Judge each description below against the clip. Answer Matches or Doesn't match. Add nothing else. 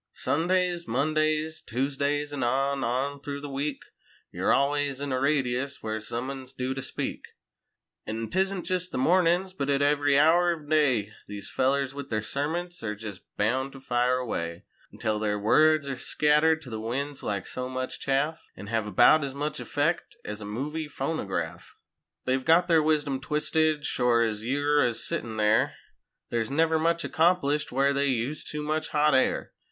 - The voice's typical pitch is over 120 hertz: Matches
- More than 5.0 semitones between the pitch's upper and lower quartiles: Doesn't match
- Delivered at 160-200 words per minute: Matches